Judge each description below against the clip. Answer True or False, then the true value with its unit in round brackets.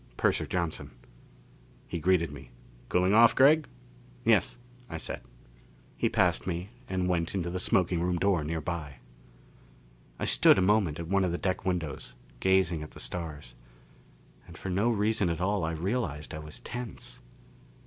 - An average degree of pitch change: True (3.0 semitones)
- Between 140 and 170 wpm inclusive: True (160 wpm)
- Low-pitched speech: True (90 Hz)